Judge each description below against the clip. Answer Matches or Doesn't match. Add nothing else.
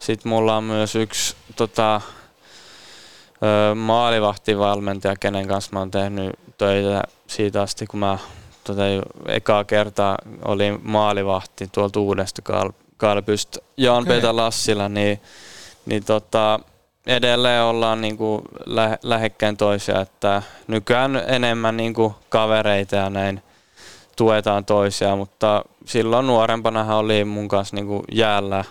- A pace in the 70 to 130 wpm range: Matches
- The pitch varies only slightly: Matches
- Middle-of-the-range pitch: Doesn't match